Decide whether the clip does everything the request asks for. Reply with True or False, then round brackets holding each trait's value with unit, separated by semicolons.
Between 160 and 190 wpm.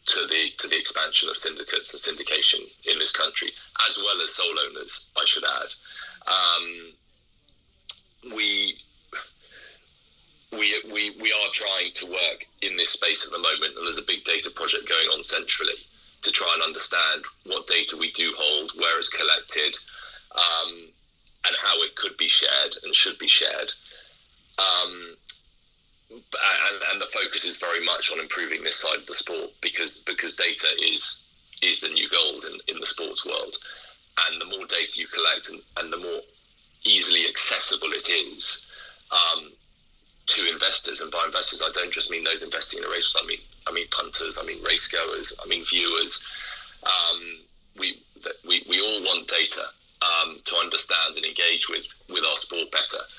True (170 wpm)